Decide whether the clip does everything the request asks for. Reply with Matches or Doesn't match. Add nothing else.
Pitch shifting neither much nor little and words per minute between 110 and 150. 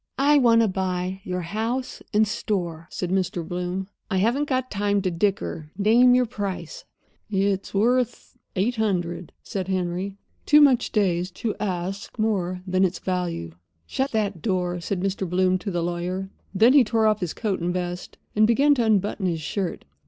Doesn't match